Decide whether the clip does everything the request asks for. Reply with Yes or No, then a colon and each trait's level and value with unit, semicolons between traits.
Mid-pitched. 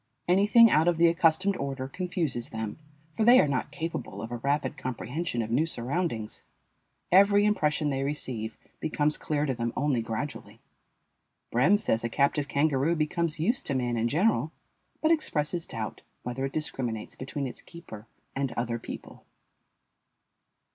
Yes: medium, 145 Hz